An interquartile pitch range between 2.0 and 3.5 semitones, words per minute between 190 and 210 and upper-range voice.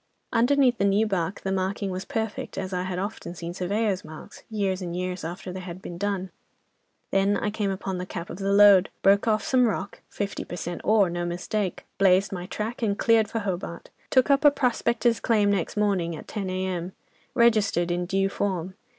Yes: average, 2.7 semitones; average, 200 wpm; high, 195 Hz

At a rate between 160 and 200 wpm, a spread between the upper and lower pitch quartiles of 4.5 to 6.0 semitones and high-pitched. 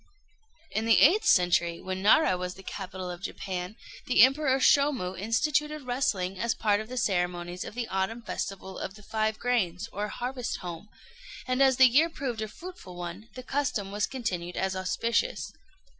Yes: average, 175 wpm; wide, 5.5 semitones; high, 215 Hz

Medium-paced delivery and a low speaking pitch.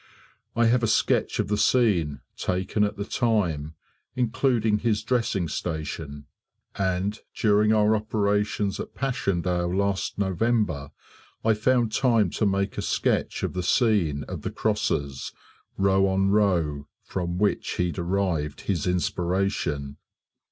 No: slow, 130 wpm; low, 100 Hz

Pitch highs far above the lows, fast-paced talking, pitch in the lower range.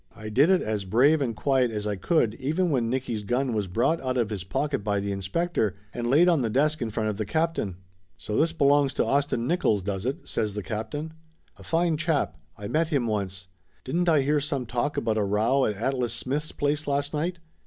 Yes: wide, 5.9 semitones; fast, 220 wpm; low, 130 Hz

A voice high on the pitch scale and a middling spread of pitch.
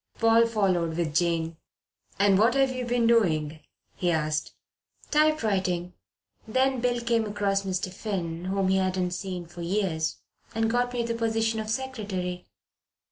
Yes: high, 195 Hz; average, 4.5 semitones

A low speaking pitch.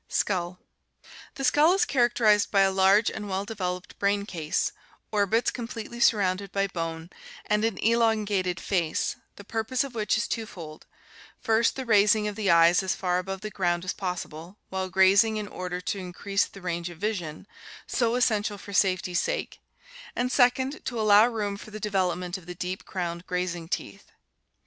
No: high, 200 Hz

